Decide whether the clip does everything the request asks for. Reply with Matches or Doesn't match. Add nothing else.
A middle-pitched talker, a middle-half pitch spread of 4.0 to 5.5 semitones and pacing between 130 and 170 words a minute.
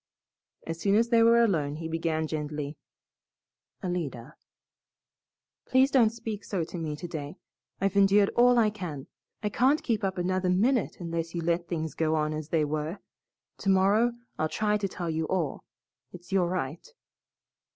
Matches